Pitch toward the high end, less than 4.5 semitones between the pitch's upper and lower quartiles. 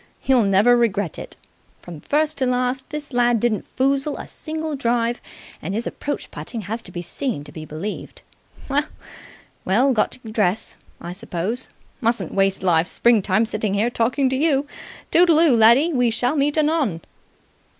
No: high, 235 Hz; average, 5.3 semitones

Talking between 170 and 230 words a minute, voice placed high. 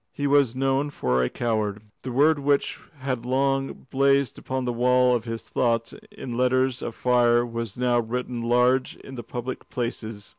No: average, 175 wpm; low, 125 Hz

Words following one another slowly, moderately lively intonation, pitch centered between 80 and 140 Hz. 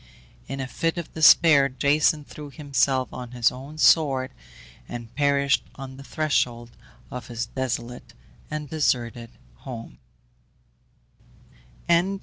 Yes: slow, 115 wpm; average, 3.3 semitones; low, 135 Hz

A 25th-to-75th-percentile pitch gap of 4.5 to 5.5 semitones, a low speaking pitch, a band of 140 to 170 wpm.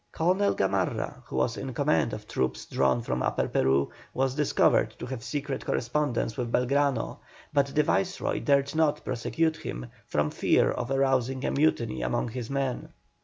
Yes: average, 4.9 semitones; low, 130 Hz; average, 165 wpm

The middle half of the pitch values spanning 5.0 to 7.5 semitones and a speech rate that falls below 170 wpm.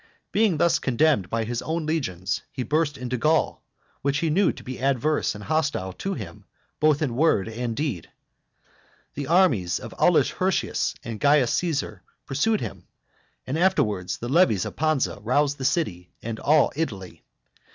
Yes: wide, 5.6 semitones; average, 160 wpm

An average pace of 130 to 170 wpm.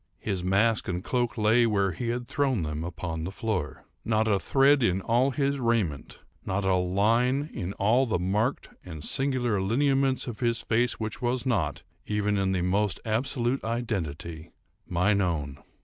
Yes: average, 165 wpm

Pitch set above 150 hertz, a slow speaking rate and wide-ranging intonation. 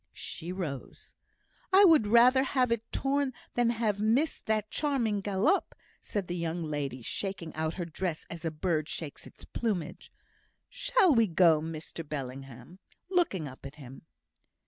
No: high, 190 Hz; average, 155 wpm; wide, 7.1 semitones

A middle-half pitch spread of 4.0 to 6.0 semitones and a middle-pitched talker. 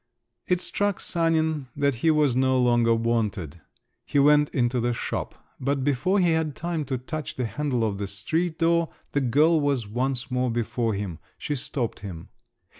No: average, 4.9 semitones; low, 130 Hz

